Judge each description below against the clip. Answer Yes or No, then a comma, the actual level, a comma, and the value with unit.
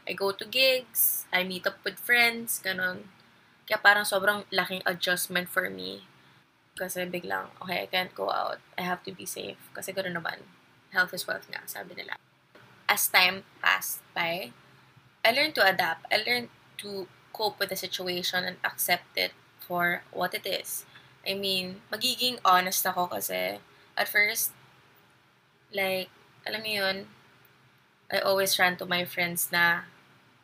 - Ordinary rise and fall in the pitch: No, narrow, 1.8 semitones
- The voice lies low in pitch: No, medium, 185 Hz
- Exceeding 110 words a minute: Yes, fast, 155 wpm